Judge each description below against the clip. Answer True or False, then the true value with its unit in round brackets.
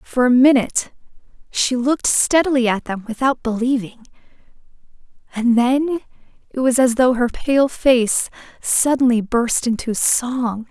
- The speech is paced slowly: True (130 wpm)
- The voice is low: False (250 Hz)